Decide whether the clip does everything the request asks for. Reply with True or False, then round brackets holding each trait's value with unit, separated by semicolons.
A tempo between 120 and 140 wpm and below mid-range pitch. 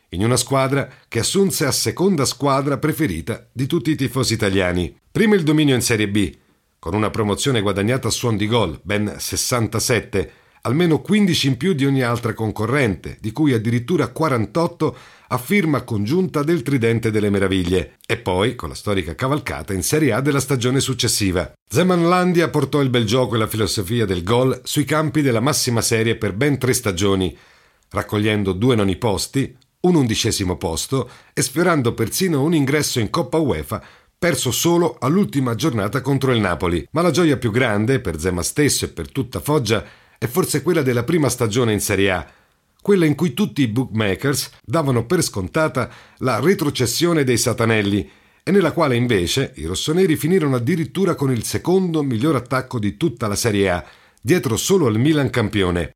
False (170 wpm; 125 Hz)